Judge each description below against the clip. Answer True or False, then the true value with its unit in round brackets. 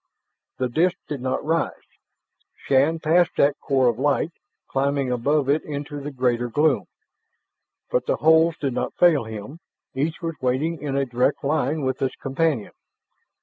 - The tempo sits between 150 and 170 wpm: True (155 wpm)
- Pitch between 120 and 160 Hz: True (140 Hz)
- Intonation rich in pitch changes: False (3.3 semitones)